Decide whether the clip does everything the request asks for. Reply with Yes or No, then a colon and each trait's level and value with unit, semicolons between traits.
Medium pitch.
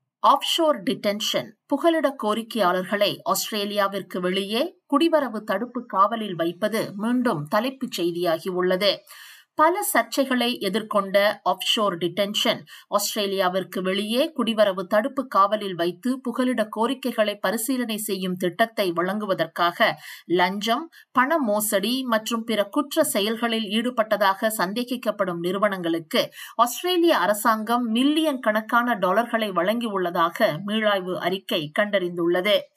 No: high, 215 Hz